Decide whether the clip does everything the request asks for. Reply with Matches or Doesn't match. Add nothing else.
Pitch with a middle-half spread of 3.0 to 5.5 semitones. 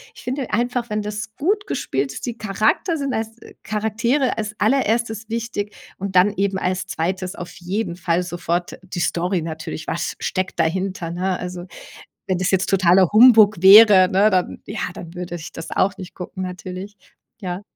Matches